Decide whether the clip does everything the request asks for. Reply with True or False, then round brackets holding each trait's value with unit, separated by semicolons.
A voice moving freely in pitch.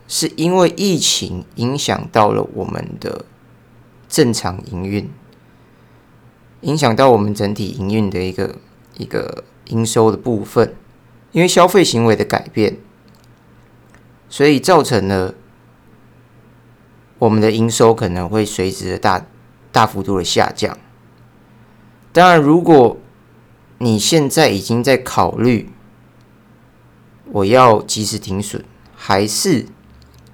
False (3.8 semitones)